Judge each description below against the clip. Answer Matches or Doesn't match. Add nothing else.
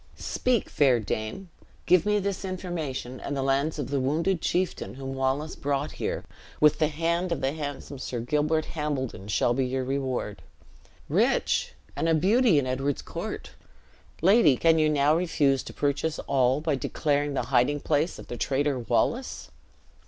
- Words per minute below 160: Doesn't match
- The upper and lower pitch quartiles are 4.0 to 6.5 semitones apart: Doesn't match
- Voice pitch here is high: Doesn't match